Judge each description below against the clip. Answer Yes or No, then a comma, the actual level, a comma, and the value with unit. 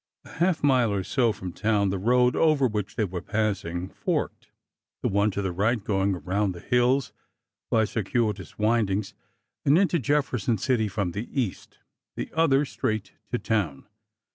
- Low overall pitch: Yes, low, 110 Hz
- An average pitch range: Yes, average, 4.3 semitones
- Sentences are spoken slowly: No, average, 165 wpm